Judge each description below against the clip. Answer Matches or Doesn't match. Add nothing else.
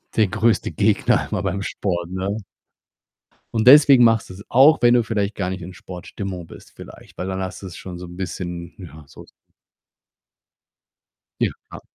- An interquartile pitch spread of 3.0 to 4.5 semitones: Matches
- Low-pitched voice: Matches